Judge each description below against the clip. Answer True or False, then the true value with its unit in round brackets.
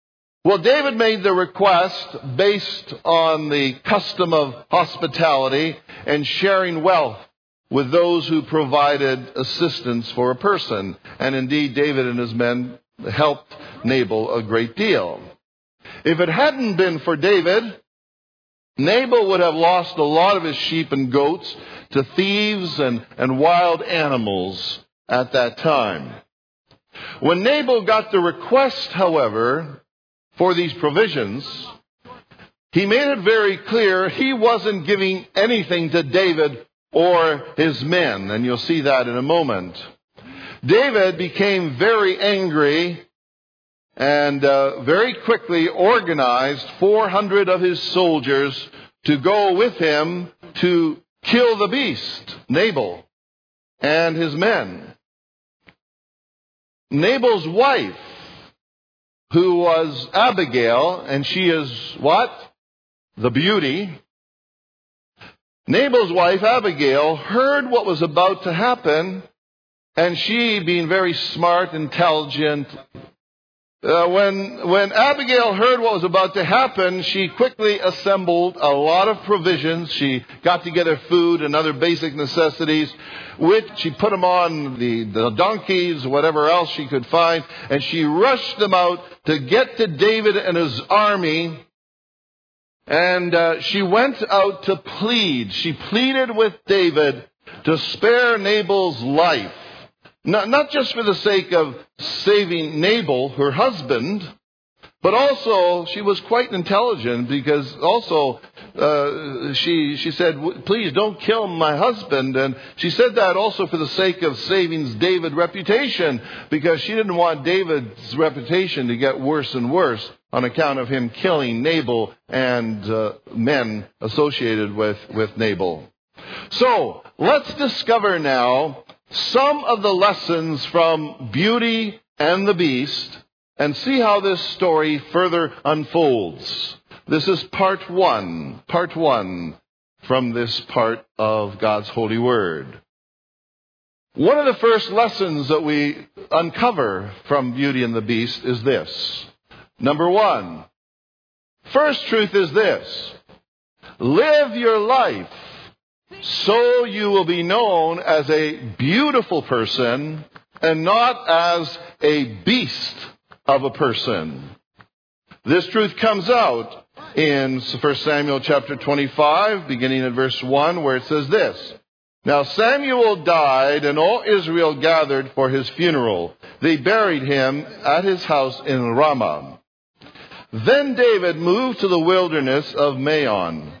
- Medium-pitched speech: True (165 Hz)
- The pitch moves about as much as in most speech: False (6.1 semitones)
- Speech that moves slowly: True (125 wpm)